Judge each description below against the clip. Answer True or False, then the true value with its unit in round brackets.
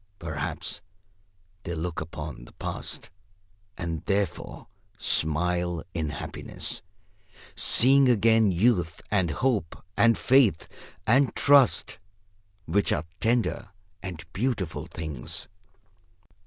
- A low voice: True (90 Hz)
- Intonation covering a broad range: True (6.2 semitones)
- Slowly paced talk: True (100 wpm)